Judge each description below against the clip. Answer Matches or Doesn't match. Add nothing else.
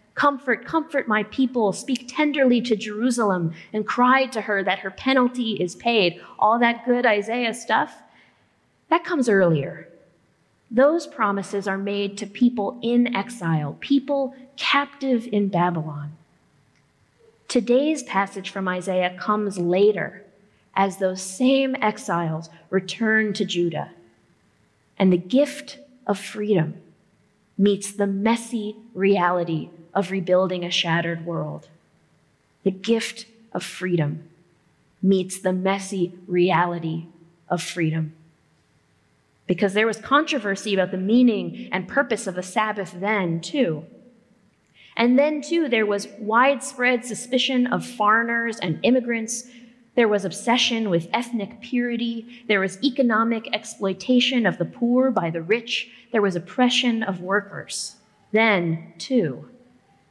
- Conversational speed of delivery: Doesn't match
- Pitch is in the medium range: Doesn't match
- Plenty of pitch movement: Doesn't match